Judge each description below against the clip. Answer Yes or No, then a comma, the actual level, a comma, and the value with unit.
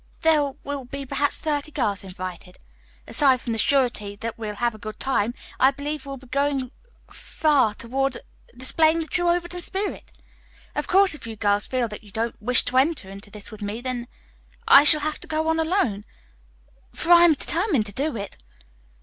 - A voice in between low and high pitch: No, very high, 265 Hz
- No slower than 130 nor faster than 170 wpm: No, average, 190 wpm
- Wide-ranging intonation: Yes, wide, 5.9 semitones